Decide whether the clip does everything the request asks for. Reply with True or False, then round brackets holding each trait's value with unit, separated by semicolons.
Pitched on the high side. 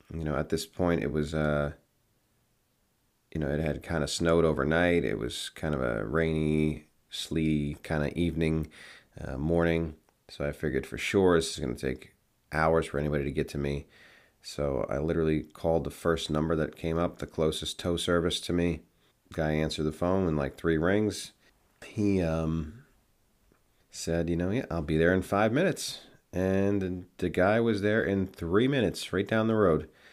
False (80 Hz)